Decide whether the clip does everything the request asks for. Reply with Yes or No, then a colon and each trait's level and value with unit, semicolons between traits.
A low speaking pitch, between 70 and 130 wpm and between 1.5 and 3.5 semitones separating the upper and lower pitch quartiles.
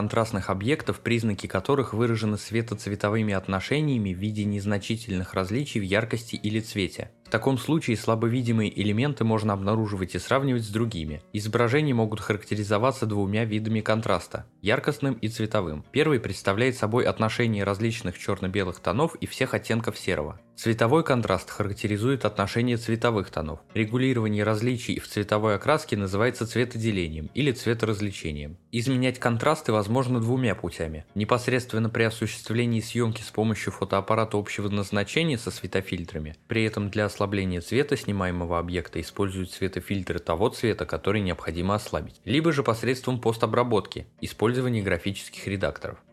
Yes: low, 110 Hz; average, 125 wpm; average, 3.2 semitones